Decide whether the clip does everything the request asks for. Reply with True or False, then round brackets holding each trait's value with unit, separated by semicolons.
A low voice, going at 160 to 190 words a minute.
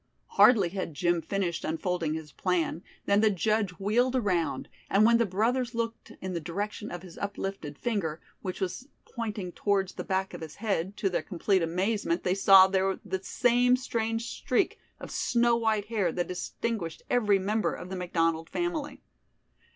False (195 Hz; 170 wpm)